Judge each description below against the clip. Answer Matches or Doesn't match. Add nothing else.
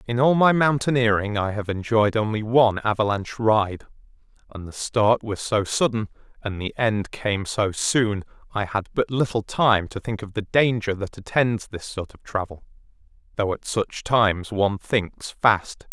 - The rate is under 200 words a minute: Matches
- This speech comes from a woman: Doesn't match